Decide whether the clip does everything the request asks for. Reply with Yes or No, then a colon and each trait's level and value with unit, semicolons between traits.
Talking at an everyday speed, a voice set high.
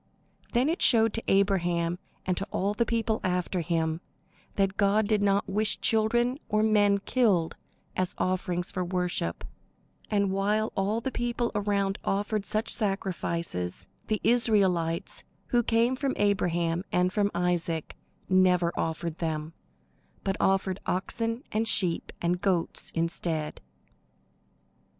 No: slow, 130 wpm; high, 195 Hz